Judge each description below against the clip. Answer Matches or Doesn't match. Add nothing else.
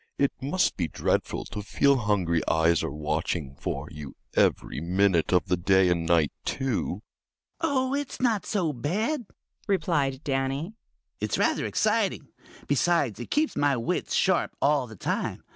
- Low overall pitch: Matches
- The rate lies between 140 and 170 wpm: Matches